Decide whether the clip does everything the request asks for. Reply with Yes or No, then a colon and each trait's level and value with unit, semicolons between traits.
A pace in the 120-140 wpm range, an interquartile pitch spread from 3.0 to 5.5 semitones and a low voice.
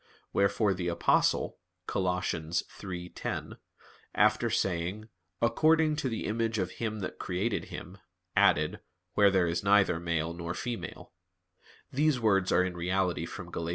Yes: slow, 135 wpm; average, 4.2 semitones; very low, 95 Hz